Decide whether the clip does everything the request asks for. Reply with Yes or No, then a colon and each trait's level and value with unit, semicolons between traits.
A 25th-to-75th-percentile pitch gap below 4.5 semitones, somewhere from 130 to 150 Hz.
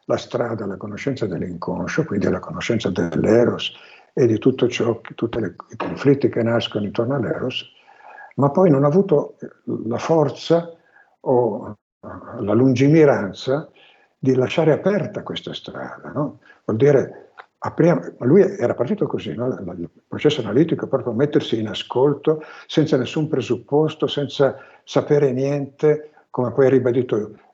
Yes: average, 3.9 semitones; medium, 140 Hz